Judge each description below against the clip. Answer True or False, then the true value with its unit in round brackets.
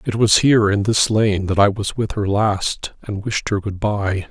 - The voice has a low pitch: True (105 Hz)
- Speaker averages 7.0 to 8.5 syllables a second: False (4.4 syllables/s)